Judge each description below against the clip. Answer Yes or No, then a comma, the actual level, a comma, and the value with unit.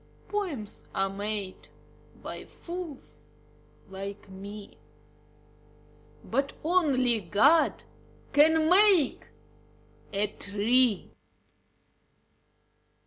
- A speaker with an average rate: No, slow, 65 wpm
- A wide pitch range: Yes, wide, 7.9 semitones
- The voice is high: Yes, high, 235 Hz